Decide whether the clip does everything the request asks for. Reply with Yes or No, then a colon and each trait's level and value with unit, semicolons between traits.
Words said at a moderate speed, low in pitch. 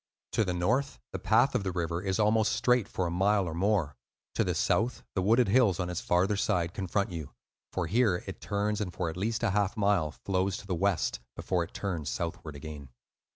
No: fast, 215 wpm; very low, 95 Hz